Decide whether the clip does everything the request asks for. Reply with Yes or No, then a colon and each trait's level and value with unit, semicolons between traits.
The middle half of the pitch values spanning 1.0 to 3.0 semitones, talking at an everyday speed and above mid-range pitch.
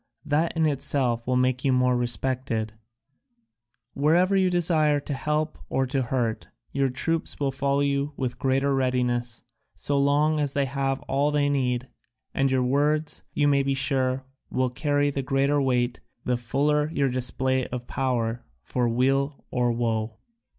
No: narrow, 2.4 semitones; average, 155 wpm; low, 135 Hz